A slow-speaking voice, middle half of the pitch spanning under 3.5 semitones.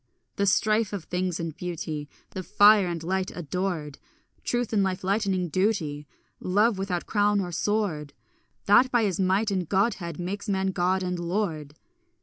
No: average, 155 wpm; average, 2.9 semitones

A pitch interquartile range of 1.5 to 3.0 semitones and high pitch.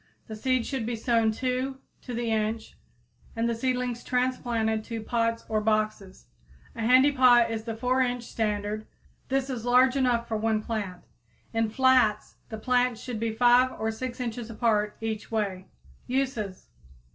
Yes: narrow, 2.4 semitones; high, 230 Hz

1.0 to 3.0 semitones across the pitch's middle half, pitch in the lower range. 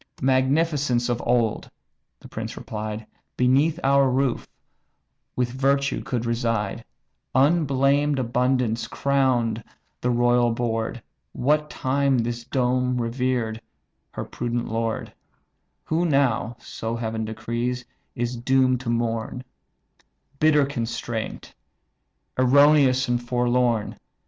Yes: narrow, 2.5 semitones; low, 125 Hz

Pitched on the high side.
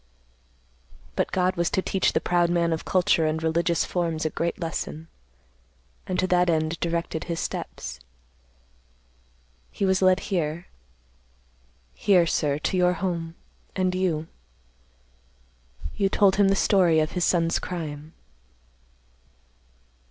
No: medium, 170 Hz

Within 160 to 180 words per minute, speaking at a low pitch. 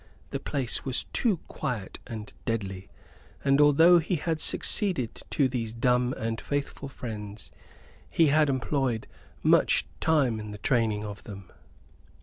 No: slow, 135 wpm; low, 125 Hz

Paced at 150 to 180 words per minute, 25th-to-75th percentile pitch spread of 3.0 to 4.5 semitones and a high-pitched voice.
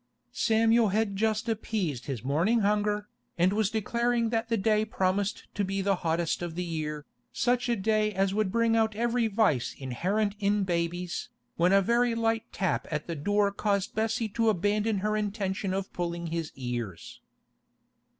Yes: average, 170 wpm; average, 3.9 semitones; high, 205 Hz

